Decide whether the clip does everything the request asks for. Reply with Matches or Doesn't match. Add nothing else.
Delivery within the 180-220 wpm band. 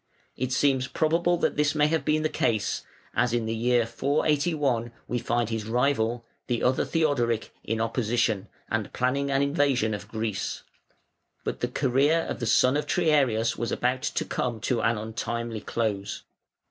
Doesn't match